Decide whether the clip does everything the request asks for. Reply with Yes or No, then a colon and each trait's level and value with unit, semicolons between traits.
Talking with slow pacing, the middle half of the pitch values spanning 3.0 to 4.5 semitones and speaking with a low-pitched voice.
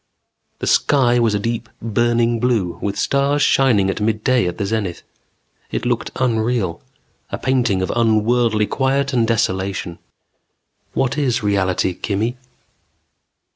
Yes: slow, 130 wpm; average, 3.6 semitones; low, 115 Hz